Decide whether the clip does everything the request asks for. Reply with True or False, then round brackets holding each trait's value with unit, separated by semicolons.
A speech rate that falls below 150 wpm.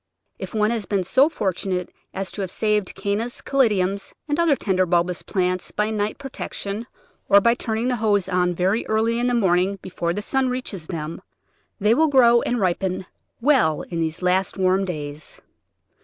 False (175 wpm)